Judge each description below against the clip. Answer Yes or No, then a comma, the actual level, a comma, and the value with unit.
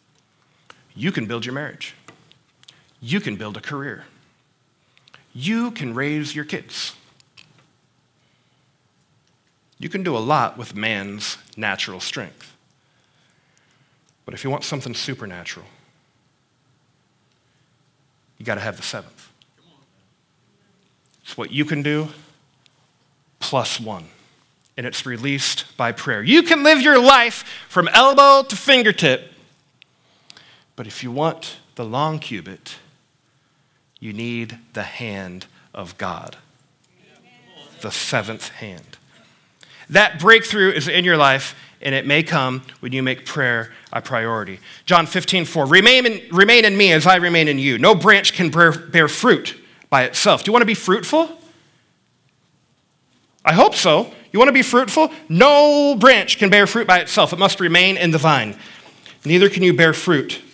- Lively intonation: Yes, wide, 7.1 semitones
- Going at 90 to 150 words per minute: Yes, average, 140 wpm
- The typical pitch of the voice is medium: Yes, medium, 155 Hz